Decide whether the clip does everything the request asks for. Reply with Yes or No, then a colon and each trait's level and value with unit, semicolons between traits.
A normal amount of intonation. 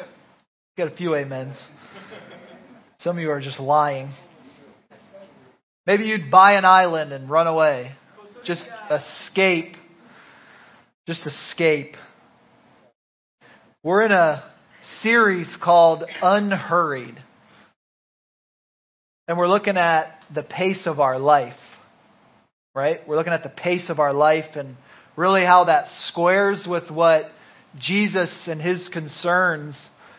Yes: average, 3.6 semitones